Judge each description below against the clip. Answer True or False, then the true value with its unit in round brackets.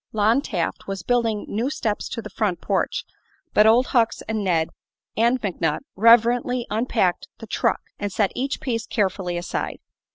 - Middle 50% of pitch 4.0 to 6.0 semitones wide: False (3.4 semitones)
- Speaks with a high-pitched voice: True (220 Hz)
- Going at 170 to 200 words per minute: False (160 wpm)